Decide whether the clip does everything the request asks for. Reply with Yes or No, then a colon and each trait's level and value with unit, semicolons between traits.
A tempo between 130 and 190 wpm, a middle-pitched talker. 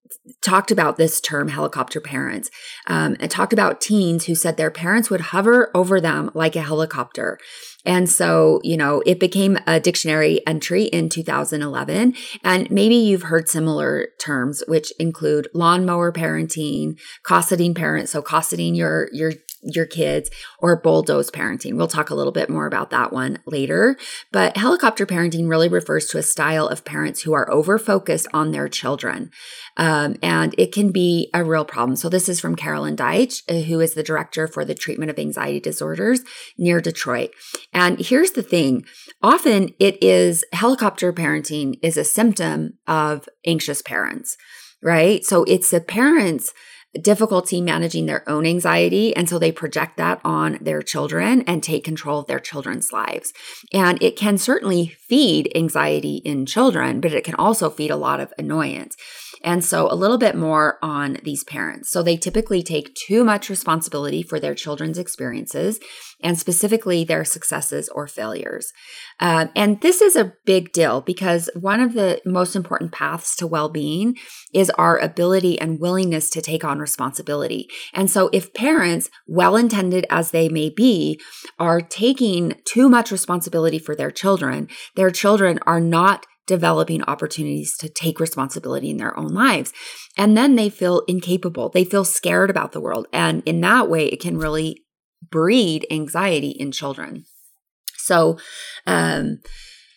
Yes: average, 165 wpm; medium, 170 Hz